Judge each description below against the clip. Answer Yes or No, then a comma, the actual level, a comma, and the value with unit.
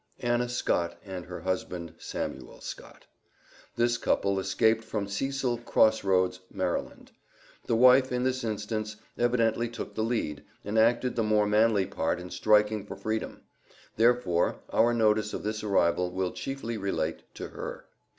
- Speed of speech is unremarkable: Yes, average, 145 wpm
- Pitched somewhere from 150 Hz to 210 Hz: No, low, 110 Hz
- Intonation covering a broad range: No, average, 3.5 semitones